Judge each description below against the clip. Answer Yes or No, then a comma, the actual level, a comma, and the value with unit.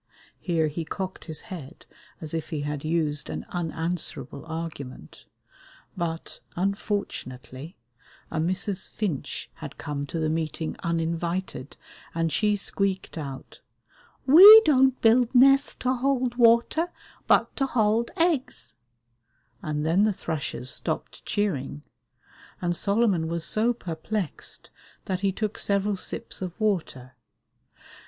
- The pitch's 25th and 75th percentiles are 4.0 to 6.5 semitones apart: Yes, average, 5.3 semitones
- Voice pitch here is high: No, medium, 175 Hz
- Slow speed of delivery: Yes, slow, 120 wpm